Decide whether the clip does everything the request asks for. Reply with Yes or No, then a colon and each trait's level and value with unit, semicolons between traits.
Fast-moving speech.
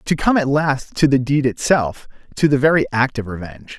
Yes: fast, 220 wpm